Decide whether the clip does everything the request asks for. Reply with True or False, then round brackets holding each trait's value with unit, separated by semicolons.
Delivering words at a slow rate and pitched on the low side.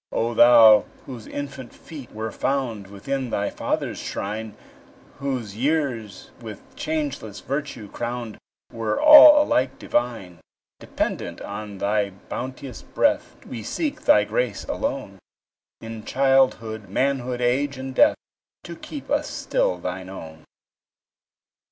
True (120 wpm; 120 Hz)